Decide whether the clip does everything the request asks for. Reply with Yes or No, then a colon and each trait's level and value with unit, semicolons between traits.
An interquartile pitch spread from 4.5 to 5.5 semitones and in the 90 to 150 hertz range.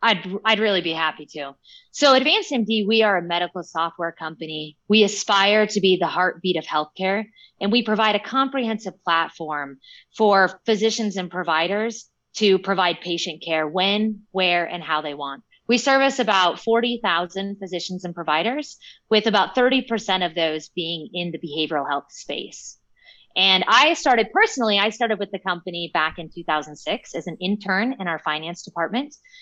No: average, 4.8 semitones; high, 190 Hz